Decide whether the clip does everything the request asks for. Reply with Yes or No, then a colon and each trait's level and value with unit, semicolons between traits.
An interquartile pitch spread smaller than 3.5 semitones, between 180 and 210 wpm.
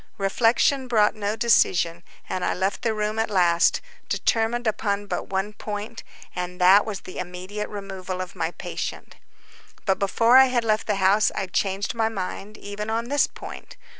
No: average, 2.9 semitones; average, 170 wpm